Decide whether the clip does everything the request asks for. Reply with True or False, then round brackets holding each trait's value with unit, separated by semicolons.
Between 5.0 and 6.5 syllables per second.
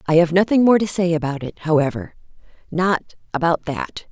True (5.8 syllables/s)